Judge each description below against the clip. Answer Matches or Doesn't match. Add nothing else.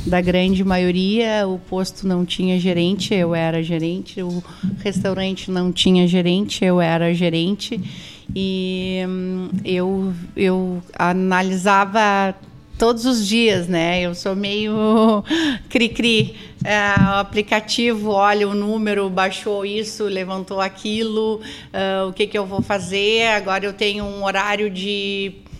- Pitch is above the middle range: Matches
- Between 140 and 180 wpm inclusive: Doesn't match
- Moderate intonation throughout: Doesn't match